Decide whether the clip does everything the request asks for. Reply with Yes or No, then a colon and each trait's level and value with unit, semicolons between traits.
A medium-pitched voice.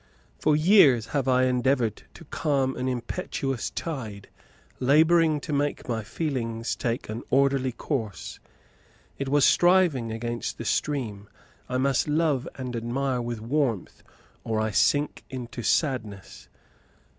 No: low, 130 Hz